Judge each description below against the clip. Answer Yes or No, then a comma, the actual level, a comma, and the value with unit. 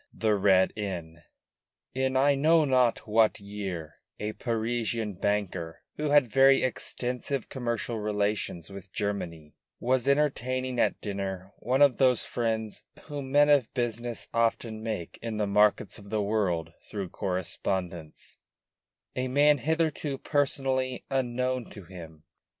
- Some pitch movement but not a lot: Yes, average, 4.7 semitones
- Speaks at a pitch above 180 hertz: No, low, 115 Hz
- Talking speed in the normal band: No, slow, 130 wpm